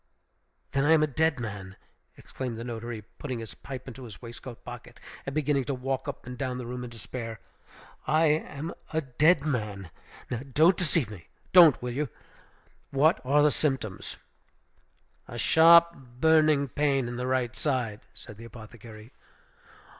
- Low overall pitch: Yes, low, 130 Hz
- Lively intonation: No, average, 4.1 semitones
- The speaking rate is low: No, average, 165 wpm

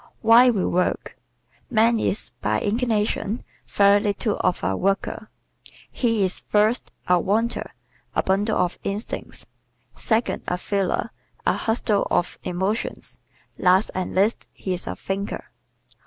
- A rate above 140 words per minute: No, slow, 135 wpm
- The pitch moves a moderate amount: Yes, average, 3.0 semitones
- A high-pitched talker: Yes, high, 205 Hz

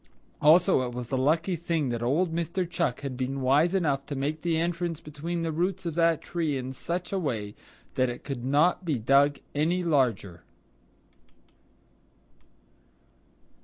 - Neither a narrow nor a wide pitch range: Yes, average, 4.4 semitones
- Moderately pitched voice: Yes, medium, 150 Hz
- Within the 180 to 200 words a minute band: No, average, 160 wpm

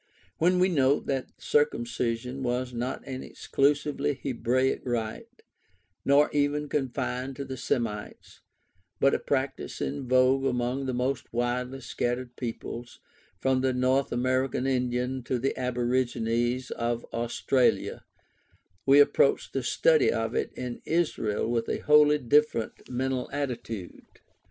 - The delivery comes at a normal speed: No, slow, 125 wpm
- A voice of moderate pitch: No, low, 130 Hz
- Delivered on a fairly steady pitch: Yes, narrow, 2.1 semitones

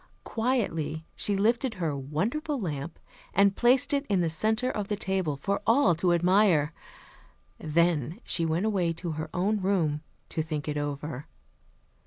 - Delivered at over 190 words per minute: No, average, 155 wpm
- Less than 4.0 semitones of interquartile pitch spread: No, average, 5.2 semitones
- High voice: No, medium, 175 Hz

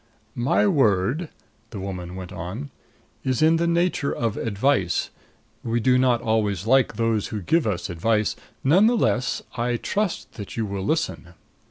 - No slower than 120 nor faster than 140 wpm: No, average, 160 wpm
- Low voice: Yes, low, 115 Hz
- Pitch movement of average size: No, wide, 6.1 semitones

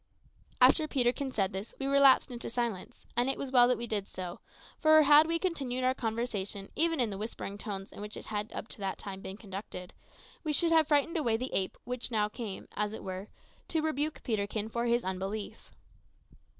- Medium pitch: No, high, 235 Hz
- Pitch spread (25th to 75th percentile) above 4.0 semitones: Yes, average, 5.3 semitones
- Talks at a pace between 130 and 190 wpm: No, fast, 205 wpm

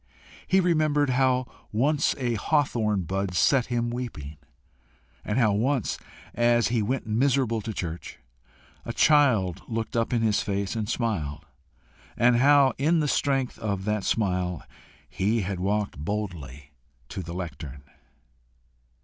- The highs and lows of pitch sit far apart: No, average, 5.0 semitones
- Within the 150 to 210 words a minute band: No, slow, 135 wpm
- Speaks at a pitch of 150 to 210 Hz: No, low, 110 Hz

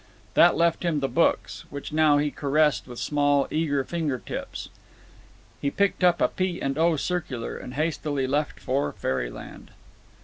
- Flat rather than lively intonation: No, average, 3.2 semitones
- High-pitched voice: No, medium, 145 Hz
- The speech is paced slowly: No, average, 160 wpm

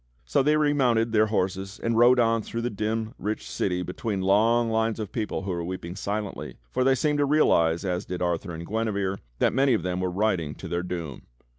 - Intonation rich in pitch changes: No, average, 4.2 semitones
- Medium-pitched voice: No, low, 105 Hz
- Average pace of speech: No, fast, 210 wpm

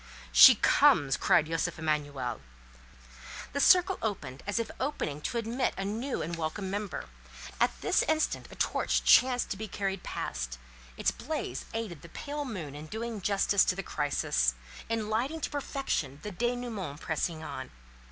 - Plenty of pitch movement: Yes, wide, 7.6 semitones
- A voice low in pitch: No, high, 195 Hz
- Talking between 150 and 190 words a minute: Yes, average, 160 wpm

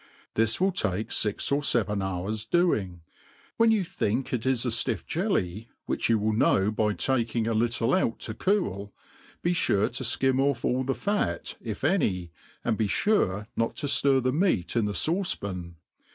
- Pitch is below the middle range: Yes, low, 115 Hz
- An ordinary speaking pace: Yes, average, 180 wpm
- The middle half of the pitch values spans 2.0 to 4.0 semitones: No, wide, 5.4 semitones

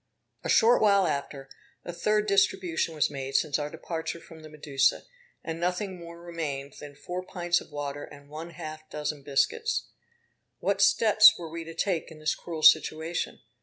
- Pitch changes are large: No, average, 3.2 semitones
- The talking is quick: No, average, 170 wpm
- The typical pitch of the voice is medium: Yes, medium, 165 Hz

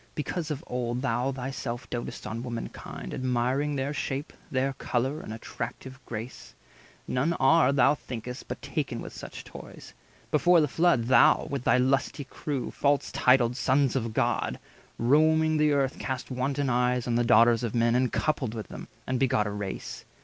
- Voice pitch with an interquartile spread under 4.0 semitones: Yes, average, 2.8 semitones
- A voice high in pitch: No, low, 130 Hz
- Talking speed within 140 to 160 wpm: No, average, 170 wpm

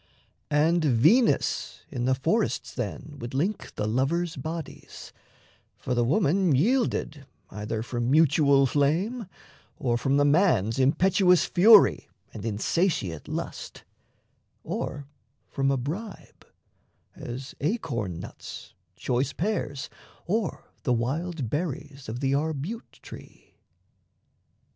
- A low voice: No, medium, 145 Hz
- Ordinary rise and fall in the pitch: No, wide, 5.7 semitones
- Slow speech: Yes, slow, 110 wpm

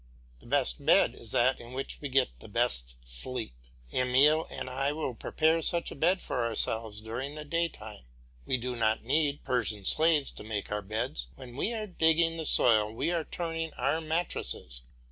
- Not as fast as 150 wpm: No, average, 185 wpm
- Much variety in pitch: Yes, wide, 6.4 semitones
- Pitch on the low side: Yes, low, 130 Hz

